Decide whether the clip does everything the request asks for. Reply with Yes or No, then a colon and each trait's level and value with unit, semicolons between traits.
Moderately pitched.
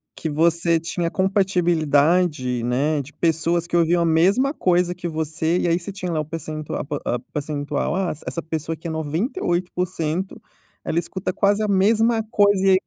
Yes: medium, 170 Hz